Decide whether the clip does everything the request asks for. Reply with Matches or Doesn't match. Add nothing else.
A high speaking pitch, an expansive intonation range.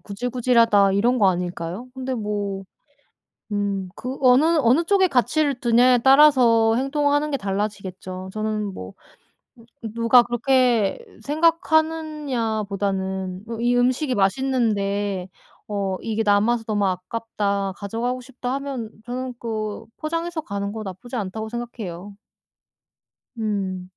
Doesn't match